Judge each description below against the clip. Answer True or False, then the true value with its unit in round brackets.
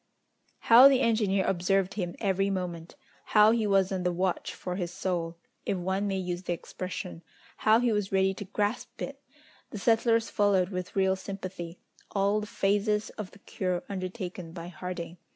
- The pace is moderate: True (170 wpm)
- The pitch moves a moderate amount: False (2.3 semitones)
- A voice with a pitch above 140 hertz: True (190 Hz)